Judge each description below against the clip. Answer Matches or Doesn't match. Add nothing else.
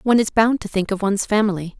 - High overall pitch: Matches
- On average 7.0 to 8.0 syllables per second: Matches